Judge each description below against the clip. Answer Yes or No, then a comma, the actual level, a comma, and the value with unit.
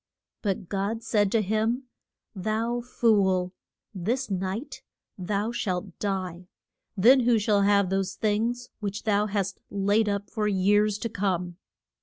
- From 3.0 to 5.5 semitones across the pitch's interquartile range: No, narrow, 2.5 semitones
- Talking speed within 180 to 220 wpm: No, slow, 135 wpm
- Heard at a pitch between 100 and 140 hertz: No, high, 205 Hz